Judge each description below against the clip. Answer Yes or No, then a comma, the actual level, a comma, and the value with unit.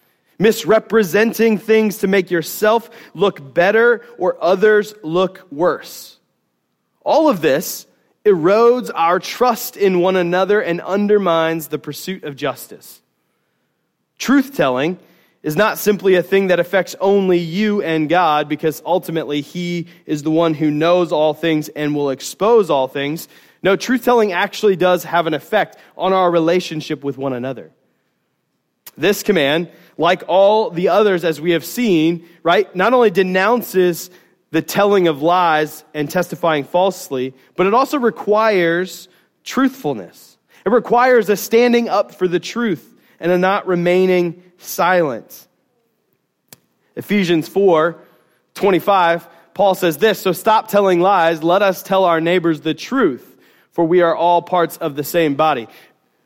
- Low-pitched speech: No, medium, 180 Hz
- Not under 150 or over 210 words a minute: No, average, 140 wpm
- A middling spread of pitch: Yes, average, 3.9 semitones